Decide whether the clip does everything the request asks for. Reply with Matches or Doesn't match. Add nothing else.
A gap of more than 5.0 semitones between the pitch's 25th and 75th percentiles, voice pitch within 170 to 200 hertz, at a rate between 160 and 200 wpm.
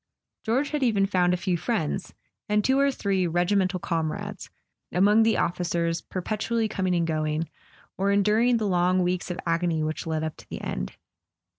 Doesn't match